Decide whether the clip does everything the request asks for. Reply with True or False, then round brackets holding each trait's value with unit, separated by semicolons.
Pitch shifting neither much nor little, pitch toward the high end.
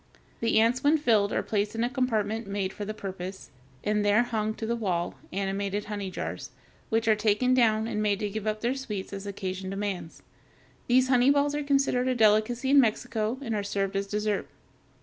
True (3.2 semitones; 215 Hz)